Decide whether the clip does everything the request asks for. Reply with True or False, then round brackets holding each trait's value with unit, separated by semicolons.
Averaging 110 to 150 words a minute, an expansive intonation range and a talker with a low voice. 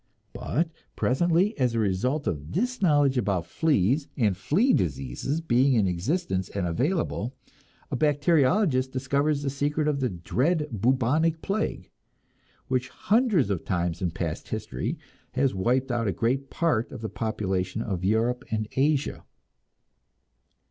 True (140 wpm; 7.1 semitones; 130 Hz)